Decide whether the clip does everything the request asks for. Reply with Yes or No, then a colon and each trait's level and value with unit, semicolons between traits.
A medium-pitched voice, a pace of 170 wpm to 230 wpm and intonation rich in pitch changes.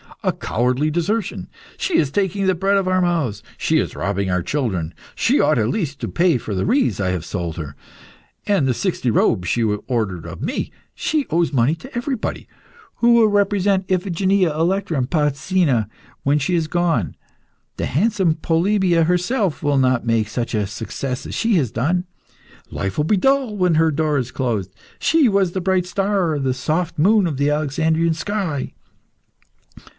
Yes: medium, 160 Hz; average, 180 wpm; wide, 7.3 semitones